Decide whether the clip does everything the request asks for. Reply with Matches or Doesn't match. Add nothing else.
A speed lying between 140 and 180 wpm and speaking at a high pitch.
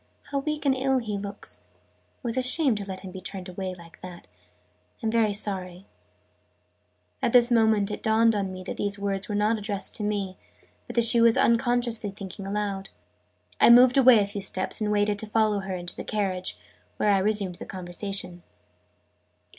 Doesn't match